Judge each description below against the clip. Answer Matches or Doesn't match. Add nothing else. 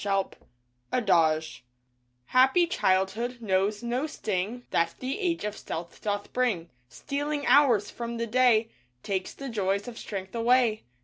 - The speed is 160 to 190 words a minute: Doesn't match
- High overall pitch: Matches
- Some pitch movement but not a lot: Matches